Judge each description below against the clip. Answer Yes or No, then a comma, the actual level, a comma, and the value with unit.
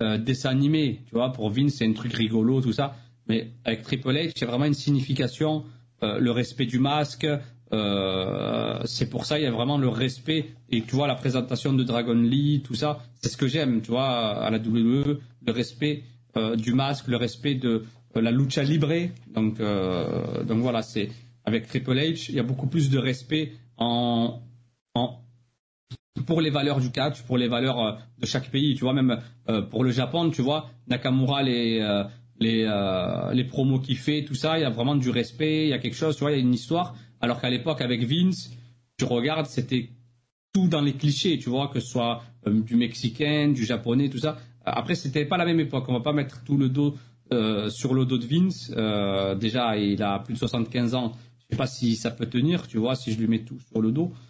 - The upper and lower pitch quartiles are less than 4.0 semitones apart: Yes, average, 3.1 semitones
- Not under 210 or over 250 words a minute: Yes, fast, 220 wpm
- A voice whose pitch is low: Yes, low, 125 Hz